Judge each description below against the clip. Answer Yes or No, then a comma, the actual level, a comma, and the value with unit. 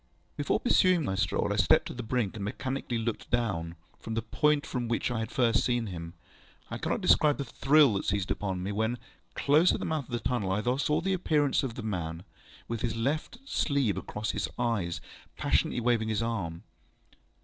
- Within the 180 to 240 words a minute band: Yes, fast, 205 wpm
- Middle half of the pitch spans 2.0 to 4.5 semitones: No, average, 5.1 semitones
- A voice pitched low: Yes, low, 115 Hz